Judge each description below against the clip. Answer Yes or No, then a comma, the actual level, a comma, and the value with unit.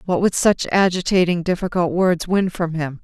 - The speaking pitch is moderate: Yes, medium, 175 Hz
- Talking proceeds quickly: No, average, 180 wpm